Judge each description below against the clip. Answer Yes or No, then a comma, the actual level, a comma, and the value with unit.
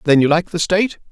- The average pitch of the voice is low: No, medium, 170 Hz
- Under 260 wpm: No, fast, 270 wpm